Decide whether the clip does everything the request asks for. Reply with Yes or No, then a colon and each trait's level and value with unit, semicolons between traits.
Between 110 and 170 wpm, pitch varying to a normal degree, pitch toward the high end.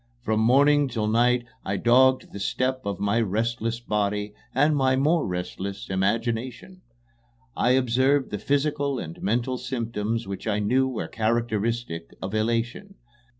No: average, 140 wpm; average, 3.9 semitones; low, 115 Hz